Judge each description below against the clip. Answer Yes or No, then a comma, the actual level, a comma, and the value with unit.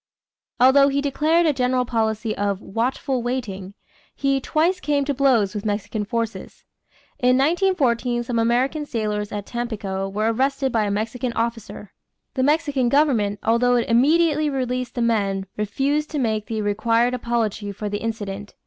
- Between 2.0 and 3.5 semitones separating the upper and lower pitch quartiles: No, average, 4.3 semitones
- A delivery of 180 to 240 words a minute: No, average, 155 wpm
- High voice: Yes, high, 240 Hz